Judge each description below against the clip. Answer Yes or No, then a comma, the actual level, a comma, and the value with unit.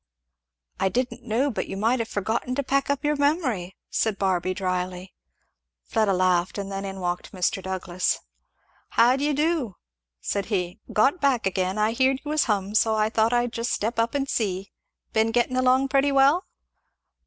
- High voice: Yes, high, 220 Hz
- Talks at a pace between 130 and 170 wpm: No, average, 180 wpm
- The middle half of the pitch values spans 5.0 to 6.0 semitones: Yes, wide, 5.6 semitones